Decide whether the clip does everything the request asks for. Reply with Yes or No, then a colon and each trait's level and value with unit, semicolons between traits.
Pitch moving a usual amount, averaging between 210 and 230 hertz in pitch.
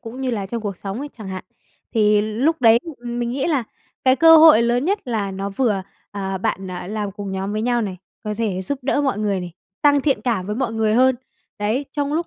Yes: average, 4.7 semitones; high, 225 Hz